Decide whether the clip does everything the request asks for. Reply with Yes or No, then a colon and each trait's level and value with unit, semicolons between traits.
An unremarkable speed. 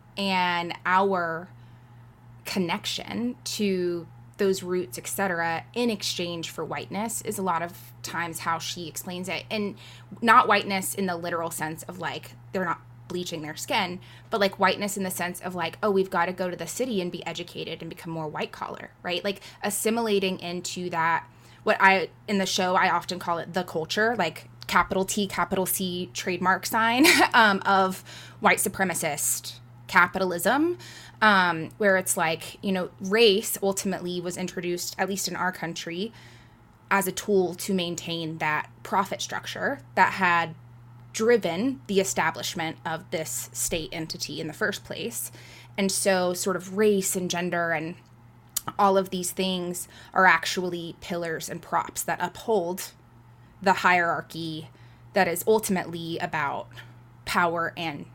Yes: average, 155 wpm